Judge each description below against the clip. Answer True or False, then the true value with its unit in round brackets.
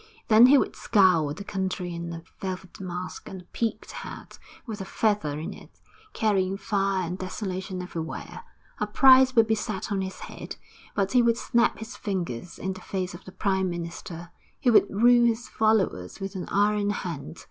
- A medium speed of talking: True (185 wpm)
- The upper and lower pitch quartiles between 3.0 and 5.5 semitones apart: True (3.3 semitones)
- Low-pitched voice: False (190 Hz)